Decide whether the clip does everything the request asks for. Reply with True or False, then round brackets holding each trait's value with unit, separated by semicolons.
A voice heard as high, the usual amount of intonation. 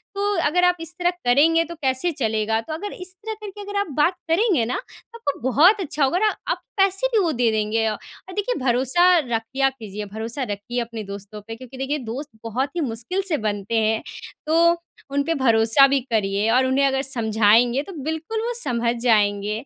False (265 Hz; 6.9 semitones)